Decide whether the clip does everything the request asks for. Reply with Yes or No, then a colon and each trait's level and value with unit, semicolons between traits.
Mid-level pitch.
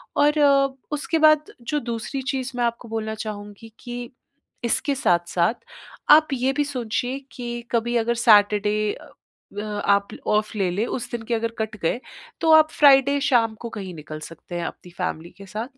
No: high, 230 Hz